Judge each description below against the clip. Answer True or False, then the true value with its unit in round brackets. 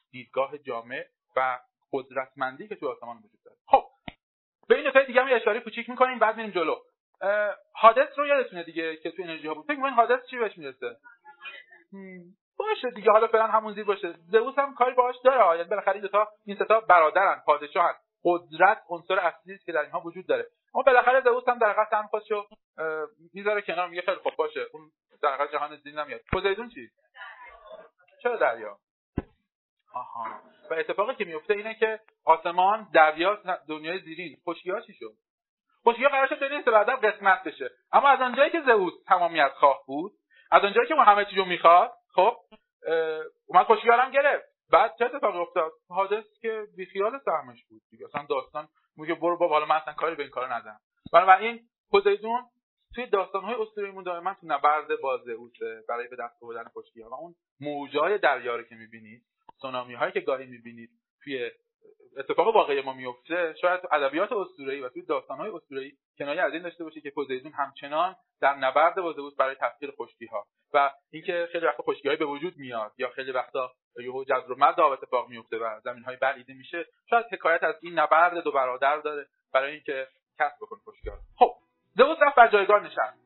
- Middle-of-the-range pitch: False (195 Hz)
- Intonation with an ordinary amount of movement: False (7.9 semitones)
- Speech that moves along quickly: True (180 wpm)